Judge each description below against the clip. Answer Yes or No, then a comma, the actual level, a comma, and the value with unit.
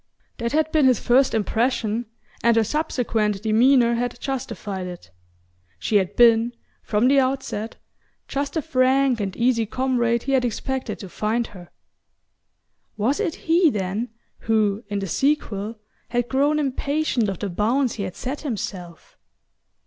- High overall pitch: Yes, high, 235 Hz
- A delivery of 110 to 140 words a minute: No, average, 150 wpm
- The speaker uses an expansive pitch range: No, average, 4.1 semitones